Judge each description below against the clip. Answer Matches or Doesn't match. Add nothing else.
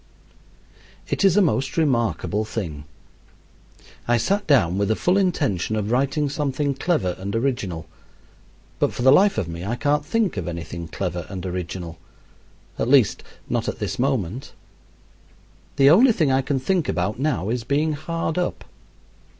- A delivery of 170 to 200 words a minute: Doesn't match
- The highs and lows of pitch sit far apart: Matches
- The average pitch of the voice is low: Matches